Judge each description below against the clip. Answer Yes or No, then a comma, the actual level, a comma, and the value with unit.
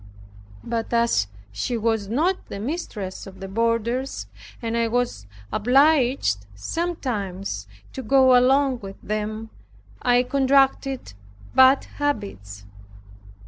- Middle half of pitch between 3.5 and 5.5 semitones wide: Yes, average, 5.0 semitones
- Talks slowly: Yes, slow, 105 wpm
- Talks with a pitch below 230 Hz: No, high, 235 Hz